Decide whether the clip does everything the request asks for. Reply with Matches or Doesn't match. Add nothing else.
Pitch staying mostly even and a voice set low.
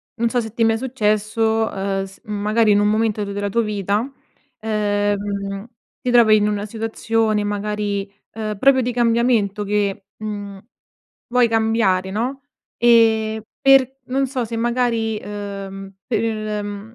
Doesn't match